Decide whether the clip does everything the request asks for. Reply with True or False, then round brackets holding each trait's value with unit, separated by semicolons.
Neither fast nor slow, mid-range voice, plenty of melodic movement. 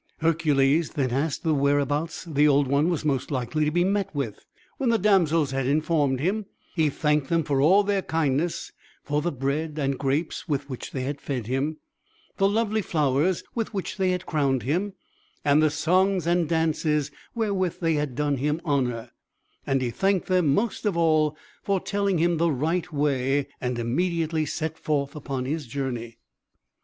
False (175 wpm; 150 Hz; 3.8 semitones)